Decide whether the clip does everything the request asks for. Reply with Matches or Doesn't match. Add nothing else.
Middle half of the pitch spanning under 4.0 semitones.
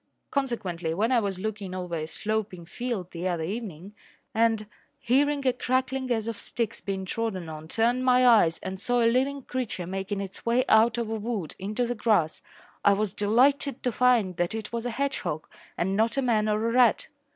Doesn't match